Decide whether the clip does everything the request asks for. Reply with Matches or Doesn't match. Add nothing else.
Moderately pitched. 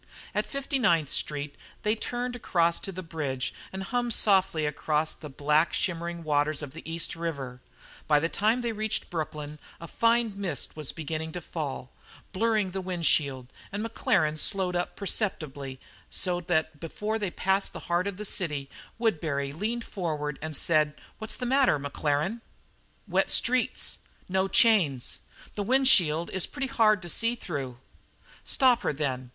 Matches